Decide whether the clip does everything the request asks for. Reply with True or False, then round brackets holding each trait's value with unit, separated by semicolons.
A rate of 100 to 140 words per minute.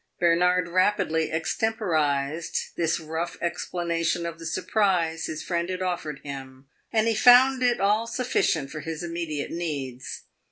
True (135 wpm)